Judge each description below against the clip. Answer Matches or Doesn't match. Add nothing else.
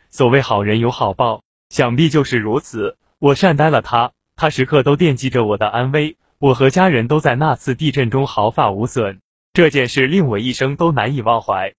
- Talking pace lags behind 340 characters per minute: Matches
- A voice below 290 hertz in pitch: Matches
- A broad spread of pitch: Doesn't match